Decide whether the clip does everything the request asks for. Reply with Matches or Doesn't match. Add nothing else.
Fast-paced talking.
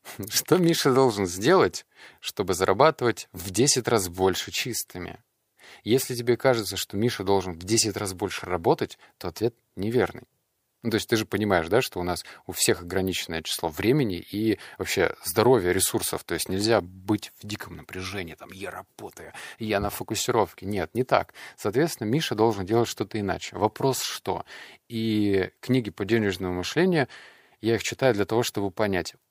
Matches